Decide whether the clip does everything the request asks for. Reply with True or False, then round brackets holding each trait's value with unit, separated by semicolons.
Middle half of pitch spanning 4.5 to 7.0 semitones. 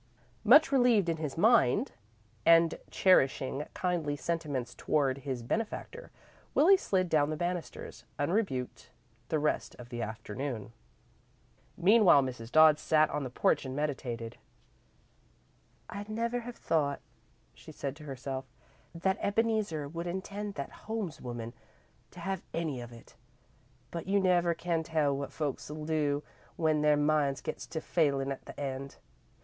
True (5.1 semitones)